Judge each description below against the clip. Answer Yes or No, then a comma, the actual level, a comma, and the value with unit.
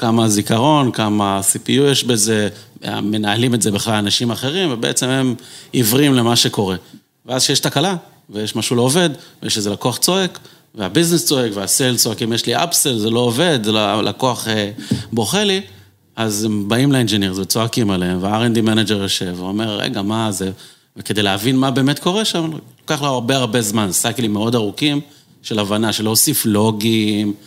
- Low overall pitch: Yes, low, 115 Hz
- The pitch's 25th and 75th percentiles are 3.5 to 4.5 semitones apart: Yes, average, 4.2 semitones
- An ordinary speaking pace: No, fast, 165 wpm